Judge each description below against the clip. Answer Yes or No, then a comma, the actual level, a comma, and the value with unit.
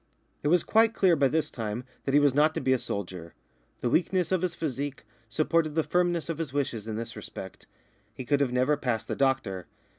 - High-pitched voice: No, medium, 140 Hz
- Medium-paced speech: No, fast, 215 wpm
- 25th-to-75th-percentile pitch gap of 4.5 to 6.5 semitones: Yes, wide, 5.4 semitones